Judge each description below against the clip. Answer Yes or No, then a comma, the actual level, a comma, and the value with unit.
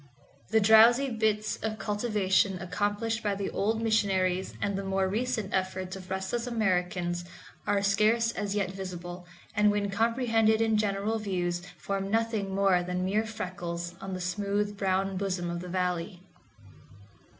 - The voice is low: No, high, 200 Hz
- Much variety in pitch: No, average, 2.8 semitones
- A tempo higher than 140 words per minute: Yes, average, 150 wpm